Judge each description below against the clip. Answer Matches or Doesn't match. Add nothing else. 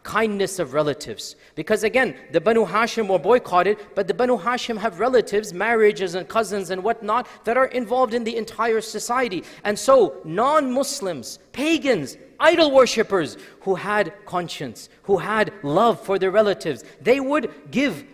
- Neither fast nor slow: Matches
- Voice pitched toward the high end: Matches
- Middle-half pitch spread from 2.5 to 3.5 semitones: Doesn't match